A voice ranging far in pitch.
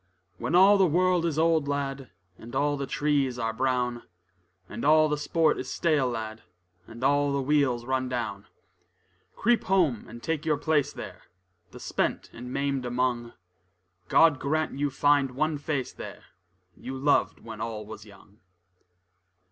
No: average, 3.8 semitones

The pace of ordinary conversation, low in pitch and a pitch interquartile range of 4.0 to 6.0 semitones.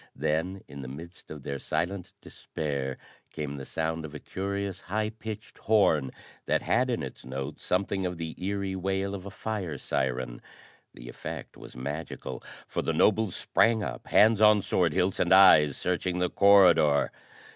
Yes: average, 165 wpm; very low, 90 Hz; average, 5.1 semitones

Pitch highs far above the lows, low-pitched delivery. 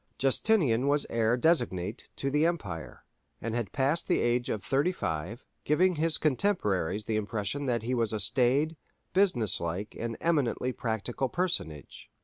Yes: wide, 5.8 semitones; low, 120 Hz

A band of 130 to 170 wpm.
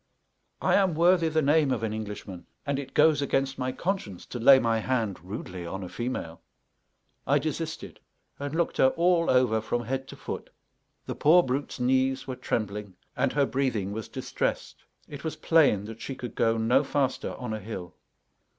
No: average, 180 wpm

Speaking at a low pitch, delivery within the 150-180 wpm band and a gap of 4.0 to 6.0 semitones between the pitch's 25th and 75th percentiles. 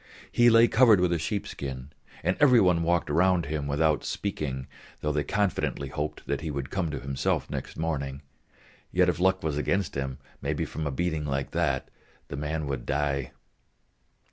Yes: very low, 75 Hz; average, 175 wpm; average, 4.4 semitones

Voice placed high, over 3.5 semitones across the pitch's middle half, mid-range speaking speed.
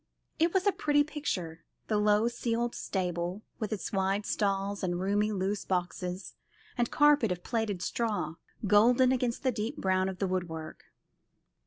Yes: high, 205 Hz; average, 4.2 semitones; average, 160 wpm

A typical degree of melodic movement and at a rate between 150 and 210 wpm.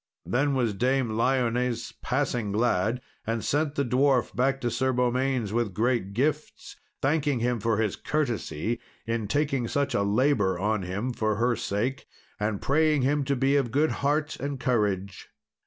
Yes: average, 3.8 semitones; average, 160 wpm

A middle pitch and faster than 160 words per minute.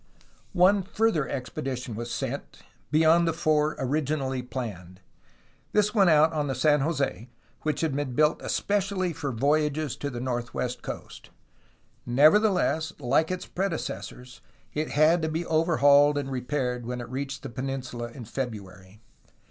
No: medium, 145 Hz; average, 145 wpm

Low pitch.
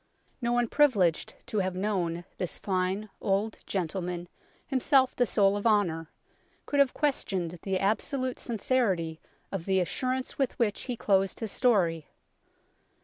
No: high, 200 Hz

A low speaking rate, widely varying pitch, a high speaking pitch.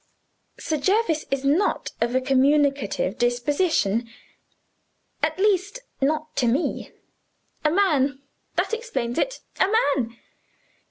Yes: slow, 110 wpm; wide, 5.7 semitones; very high, 285 Hz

